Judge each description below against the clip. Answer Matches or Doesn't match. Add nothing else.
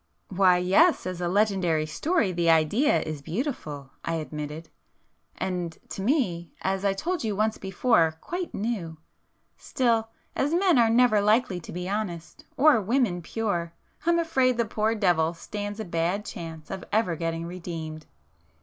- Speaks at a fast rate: Doesn't match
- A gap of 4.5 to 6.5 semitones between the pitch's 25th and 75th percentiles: Matches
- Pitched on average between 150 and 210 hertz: Matches